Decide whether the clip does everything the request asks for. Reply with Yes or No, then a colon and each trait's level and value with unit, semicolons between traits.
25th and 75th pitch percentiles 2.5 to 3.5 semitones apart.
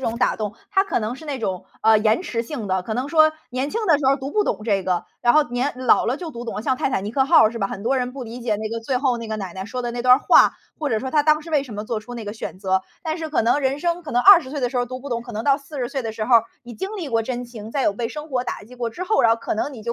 No: average, 4.1 semitones